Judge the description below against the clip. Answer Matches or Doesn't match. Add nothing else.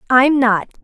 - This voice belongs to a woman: Matches